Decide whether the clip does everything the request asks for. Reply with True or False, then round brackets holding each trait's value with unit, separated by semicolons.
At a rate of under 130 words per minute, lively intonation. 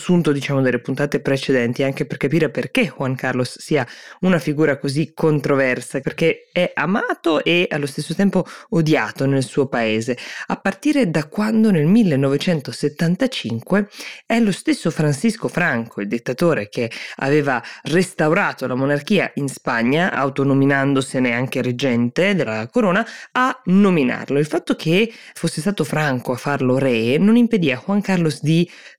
False (145 wpm; 5.7 semitones)